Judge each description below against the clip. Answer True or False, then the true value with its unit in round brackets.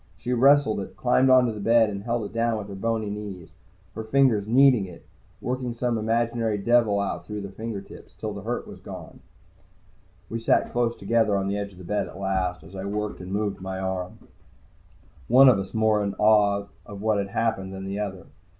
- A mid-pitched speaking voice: False (105 Hz)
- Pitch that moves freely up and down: False (3.0 semitones)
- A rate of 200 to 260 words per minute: True (205 wpm)